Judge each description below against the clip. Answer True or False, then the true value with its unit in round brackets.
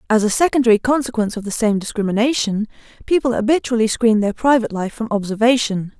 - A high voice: True (230 Hz)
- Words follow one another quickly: False (160 wpm)